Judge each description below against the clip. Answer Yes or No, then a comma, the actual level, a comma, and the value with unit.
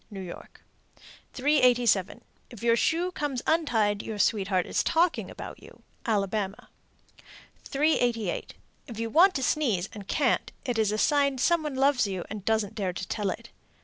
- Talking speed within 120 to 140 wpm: No, average, 160 wpm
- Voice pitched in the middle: No, high, 230 Hz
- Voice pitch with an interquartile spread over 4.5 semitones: Yes, wide, 5.5 semitones